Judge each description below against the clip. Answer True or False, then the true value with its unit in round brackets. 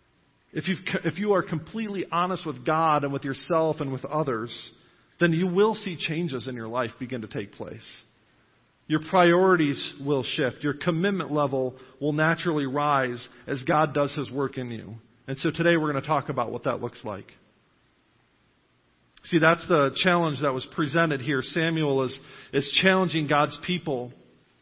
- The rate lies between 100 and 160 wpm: False (170 wpm)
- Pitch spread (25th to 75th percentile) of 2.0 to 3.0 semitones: False (4.1 semitones)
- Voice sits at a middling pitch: True (145 Hz)